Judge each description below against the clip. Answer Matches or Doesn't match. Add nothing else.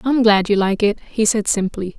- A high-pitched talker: Matches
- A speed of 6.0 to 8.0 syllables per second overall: Doesn't match